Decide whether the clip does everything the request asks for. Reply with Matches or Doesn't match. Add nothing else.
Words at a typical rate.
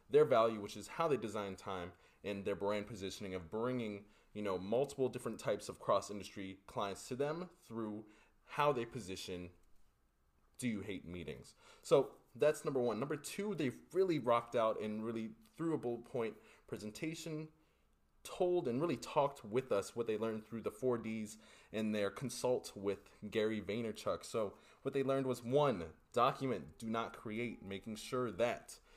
Matches